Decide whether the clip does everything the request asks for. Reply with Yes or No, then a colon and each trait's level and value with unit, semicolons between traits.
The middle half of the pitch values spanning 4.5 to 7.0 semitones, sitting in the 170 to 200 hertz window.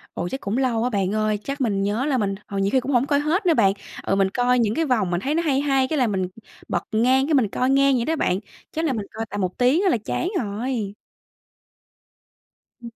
No: average, 5.1 semitones; high, 245 Hz